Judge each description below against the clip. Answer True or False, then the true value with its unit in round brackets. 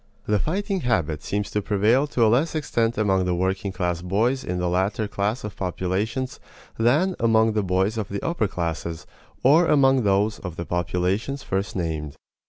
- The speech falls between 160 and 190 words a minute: True (180 wpm)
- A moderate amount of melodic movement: True (5.0 semitones)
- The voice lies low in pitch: True (105 Hz)